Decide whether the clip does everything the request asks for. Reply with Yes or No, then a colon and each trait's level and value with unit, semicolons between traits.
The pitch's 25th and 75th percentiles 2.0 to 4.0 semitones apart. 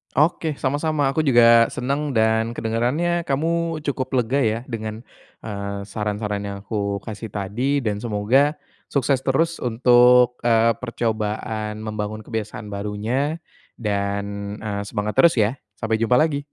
No: average, 4.4 semitones